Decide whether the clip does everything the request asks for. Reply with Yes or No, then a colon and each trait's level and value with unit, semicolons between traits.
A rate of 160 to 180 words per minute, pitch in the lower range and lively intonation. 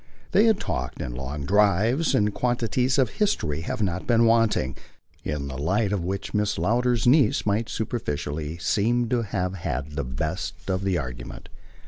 Yes: average, 165 wpm; low, 100 Hz; wide, 7.3 semitones